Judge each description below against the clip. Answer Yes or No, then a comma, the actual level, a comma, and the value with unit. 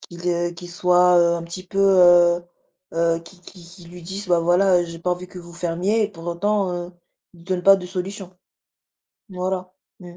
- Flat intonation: Yes, narrow, 1.4 semitones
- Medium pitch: Yes, medium, 180 Hz